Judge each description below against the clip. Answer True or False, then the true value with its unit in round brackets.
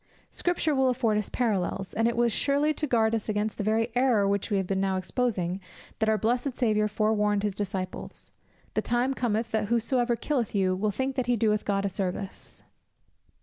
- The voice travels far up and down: False (3.2 semitones)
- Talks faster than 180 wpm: True (190 wpm)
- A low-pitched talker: False (220 Hz)